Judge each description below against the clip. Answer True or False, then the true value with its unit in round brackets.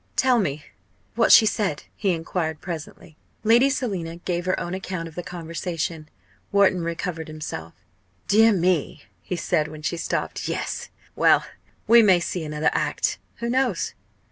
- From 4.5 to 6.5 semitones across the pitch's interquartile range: False (3.9 semitones)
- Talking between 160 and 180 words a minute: False (150 wpm)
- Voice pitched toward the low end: False (175 Hz)